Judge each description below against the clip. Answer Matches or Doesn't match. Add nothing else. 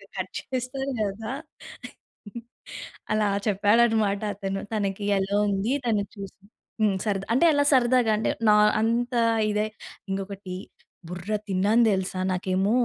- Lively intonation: Doesn't match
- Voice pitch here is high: Matches